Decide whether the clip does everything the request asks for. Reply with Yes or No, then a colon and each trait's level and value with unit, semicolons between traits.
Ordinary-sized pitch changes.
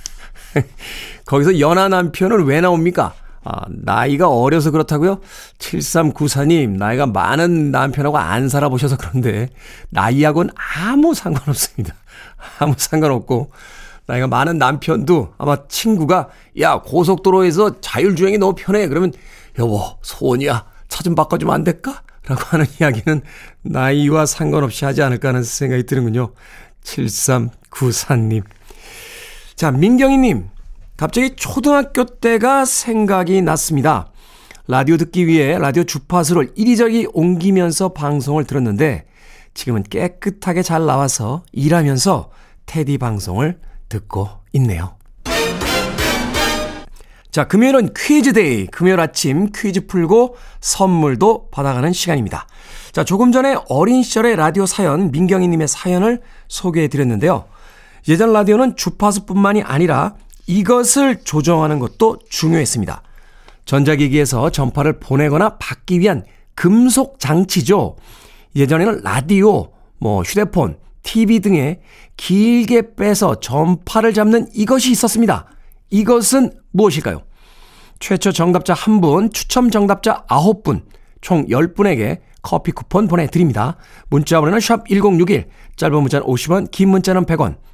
No: wide, 6.5 semitones